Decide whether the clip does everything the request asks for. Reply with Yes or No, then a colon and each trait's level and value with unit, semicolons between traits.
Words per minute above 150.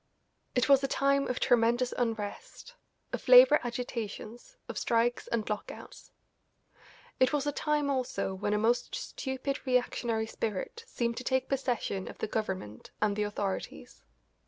No: average, 145 wpm